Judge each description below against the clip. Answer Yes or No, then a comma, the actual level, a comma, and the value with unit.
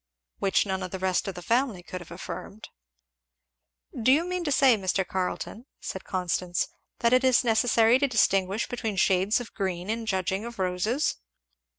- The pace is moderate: Yes, average, 175 wpm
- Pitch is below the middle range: No, high, 205 Hz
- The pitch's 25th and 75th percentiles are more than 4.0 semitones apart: Yes, average, 4.4 semitones